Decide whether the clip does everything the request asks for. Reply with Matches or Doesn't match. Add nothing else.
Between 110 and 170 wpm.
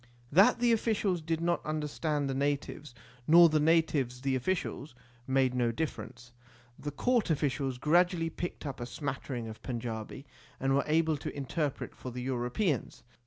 Matches